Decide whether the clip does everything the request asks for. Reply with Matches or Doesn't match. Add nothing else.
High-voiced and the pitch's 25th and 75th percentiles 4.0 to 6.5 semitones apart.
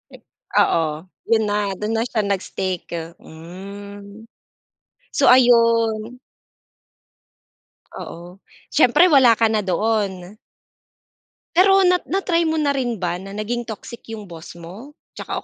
Matches